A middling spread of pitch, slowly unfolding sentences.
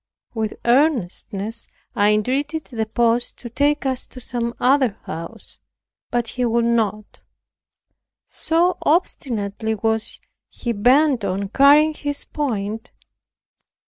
Yes: average, 4.3 semitones; slow, 110 wpm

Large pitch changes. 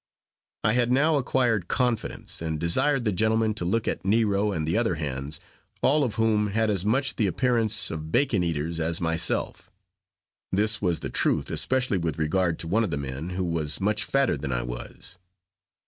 Yes: wide, 5.8 semitones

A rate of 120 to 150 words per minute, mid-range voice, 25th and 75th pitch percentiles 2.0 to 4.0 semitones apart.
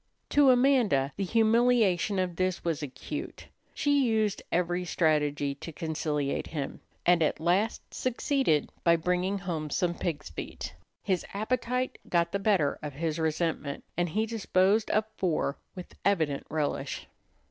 No: average, 140 wpm; medium, 180 Hz; wide, 5.5 semitones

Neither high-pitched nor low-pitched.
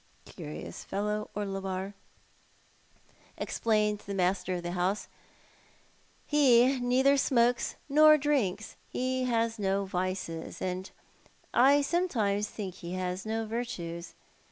No: high, 210 Hz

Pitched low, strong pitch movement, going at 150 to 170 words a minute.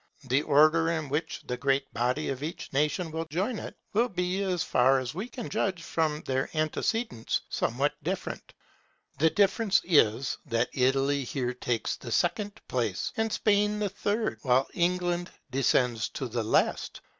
No: medium, 155 Hz; wide, 6.1 semitones; average, 160 wpm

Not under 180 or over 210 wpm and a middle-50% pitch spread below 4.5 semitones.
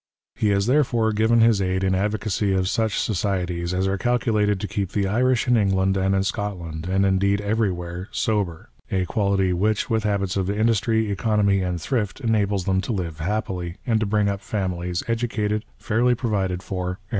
Yes: average, 190 wpm; average, 2.7 semitones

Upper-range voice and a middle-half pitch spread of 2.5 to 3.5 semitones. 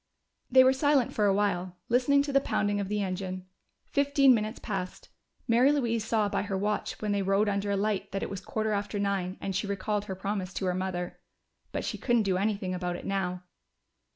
Yes: high, 205 Hz; average, 2.9 semitones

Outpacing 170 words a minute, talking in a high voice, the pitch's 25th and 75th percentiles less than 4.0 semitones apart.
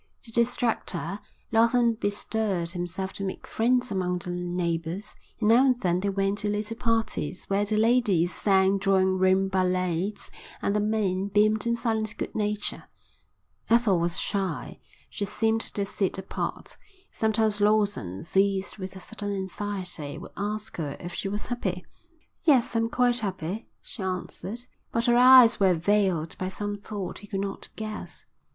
No: average, 160 wpm; high, 200 Hz; average, 2.8 semitones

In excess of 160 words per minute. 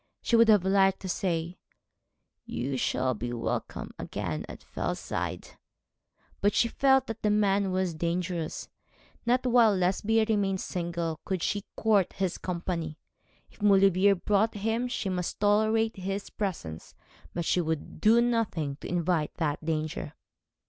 No: average, 140 wpm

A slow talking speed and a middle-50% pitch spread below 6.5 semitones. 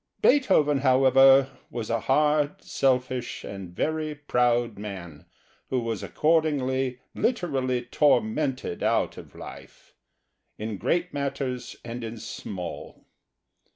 Yes: slow, 105 wpm; average, 4.1 semitones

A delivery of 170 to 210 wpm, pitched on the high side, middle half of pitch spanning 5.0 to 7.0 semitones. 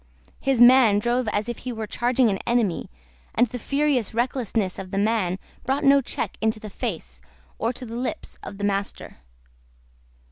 No: average, 175 wpm; high, 230 Hz; average, 3.4 semitones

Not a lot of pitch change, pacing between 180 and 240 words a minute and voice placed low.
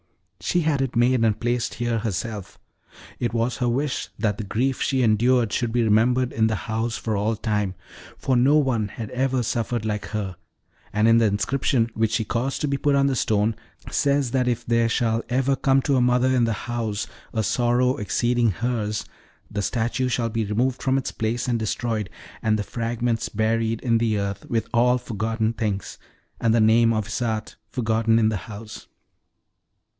Yes: narrow, 2.2 semitones; average, 185 wpm; low, 115 Hz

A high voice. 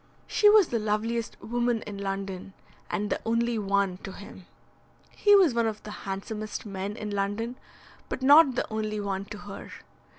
Yes: high, 210 Hz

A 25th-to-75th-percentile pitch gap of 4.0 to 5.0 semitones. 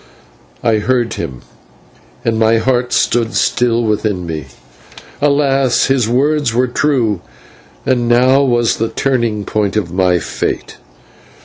No: average, 3.3 semitones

